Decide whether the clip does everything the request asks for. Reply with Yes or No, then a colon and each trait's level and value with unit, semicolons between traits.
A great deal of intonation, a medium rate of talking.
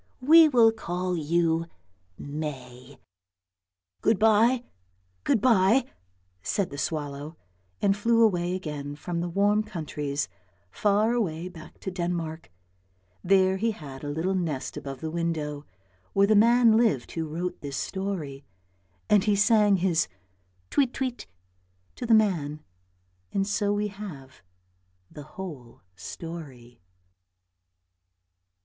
No: wide, 6.1 semitones; slow, 130 wpm